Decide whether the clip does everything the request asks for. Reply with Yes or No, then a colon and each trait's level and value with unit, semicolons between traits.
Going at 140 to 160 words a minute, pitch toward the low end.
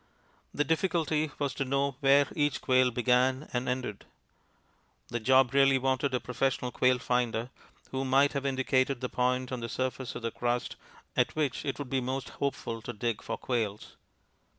No: average, 175 wpm; low, 130 Hz